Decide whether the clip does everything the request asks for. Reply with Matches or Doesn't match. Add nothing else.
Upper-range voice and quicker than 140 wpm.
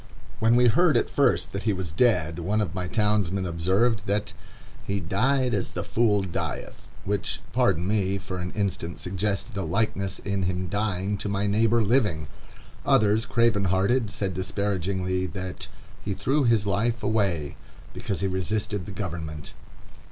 Doesn't match